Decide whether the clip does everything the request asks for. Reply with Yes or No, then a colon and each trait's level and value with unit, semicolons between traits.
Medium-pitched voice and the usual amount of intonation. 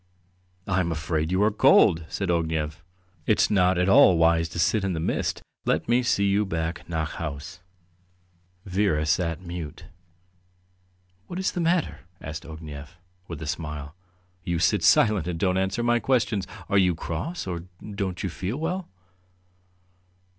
No: very low, 90 Hz; average, 3.7 semitones